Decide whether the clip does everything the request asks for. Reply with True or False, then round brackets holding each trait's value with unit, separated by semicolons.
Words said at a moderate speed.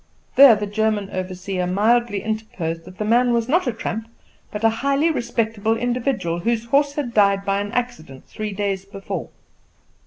True (165 wpm)